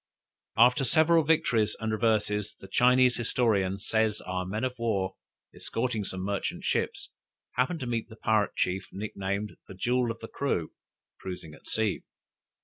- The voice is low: Yes, low, 110 Hz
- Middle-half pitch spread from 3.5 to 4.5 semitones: Yes, average, 3.9 semitones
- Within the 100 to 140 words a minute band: No, average, 150 wpm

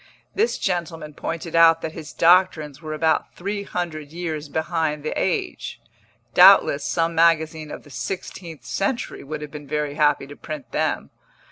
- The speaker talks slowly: No, average, 155 wpm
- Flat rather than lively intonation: Yes, narrow, 2.0 semitones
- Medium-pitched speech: Yes, medium, 160 Hz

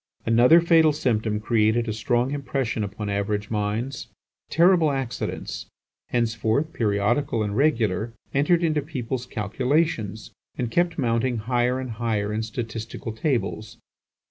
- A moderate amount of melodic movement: Yes, average, 4.1 semitones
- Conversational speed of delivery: No, slow, 120 wpm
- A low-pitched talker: Yes, low, 120 Hz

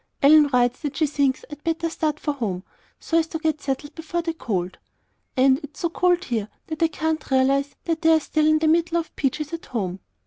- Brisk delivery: Yes, fast, 215 wpm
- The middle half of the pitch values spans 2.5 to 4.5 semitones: Yes, average, 3.3 semitones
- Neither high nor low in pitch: No, very high, 305 Hz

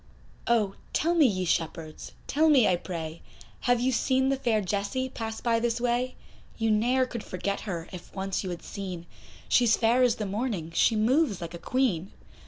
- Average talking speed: Yes, average, 190 wpm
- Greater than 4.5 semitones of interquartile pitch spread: Yes, average, 5.2 semitones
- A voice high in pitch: Yes, high, 220 Hz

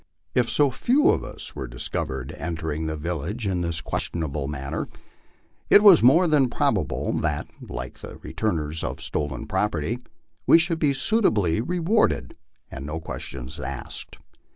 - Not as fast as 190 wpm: Yes, average, 150 wpm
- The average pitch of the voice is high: No, very low, 85 Hz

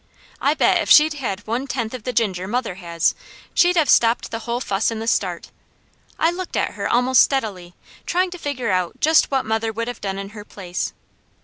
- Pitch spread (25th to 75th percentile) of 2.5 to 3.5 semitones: No, average, 5.2 semitones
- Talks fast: Yes, fast, 210 wpm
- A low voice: No, high, 230 Hz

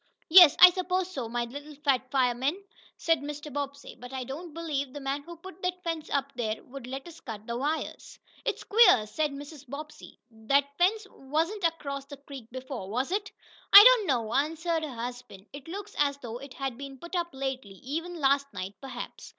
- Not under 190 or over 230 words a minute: Yes, average, 195 wpm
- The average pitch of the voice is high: Yes, very high, 280 Hz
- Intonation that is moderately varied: Yes, average, 4.2 semitones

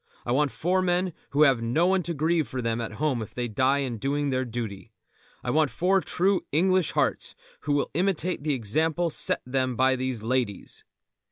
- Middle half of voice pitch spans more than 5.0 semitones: Yes, wide, 5.5 semitones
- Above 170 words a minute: Yes, average, 195 wpm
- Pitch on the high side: No, medium, 140 Hz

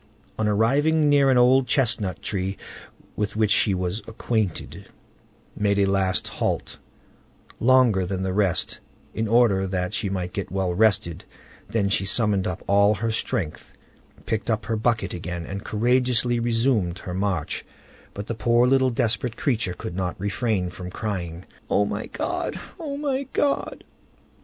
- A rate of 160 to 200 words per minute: No, average, 150 wpm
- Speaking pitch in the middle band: No, low, 105 Hz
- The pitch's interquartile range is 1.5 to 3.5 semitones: No, average, 4.0 semitones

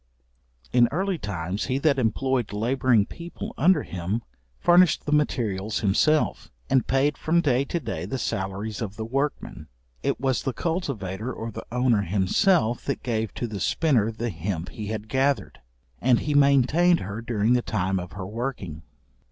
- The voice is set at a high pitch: No, low, 120 Hz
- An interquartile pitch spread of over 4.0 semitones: Yes, average, 5.3 semitones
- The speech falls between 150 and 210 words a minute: Yes, average, 165 wpm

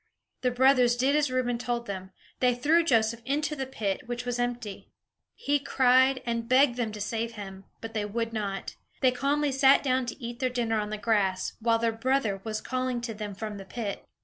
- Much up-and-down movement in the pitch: No, average, 3.0 semitones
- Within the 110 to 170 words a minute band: No, fast, 205 wpm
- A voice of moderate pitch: No, high, 240 Hz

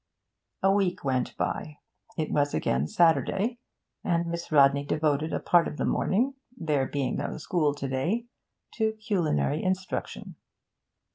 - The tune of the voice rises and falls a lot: No, average, 4.9 semitones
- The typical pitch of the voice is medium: Yes, medium, 160 Hz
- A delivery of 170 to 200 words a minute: No, average, 140 wpm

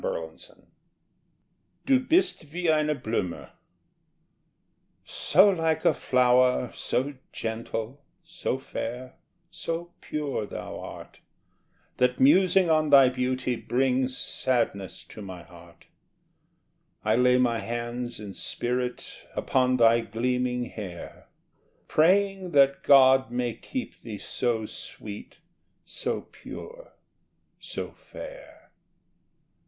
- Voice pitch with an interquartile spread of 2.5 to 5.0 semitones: Yes, average, 4.6 semitones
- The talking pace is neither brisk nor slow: No, slow, 100 wpm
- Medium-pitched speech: No, low, 125 Hz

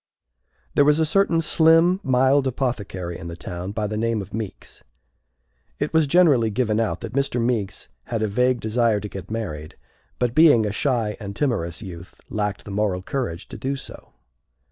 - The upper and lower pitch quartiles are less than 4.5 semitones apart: No, average, 5.1 semitones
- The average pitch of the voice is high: No, low, 115 Hz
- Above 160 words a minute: Yes, average, 180 wpm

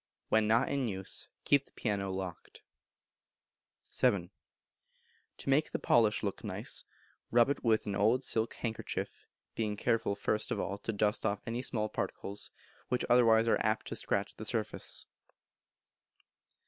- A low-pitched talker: Yes, low, 110 Hz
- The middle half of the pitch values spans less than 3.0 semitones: Yes, narrow, 2.6 semitones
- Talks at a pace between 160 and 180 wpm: No, average, 150 wpm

